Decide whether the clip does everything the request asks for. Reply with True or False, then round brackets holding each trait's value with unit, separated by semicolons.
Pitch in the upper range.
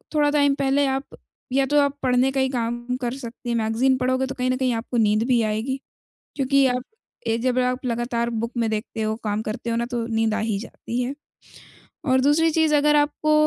True (250 Hz)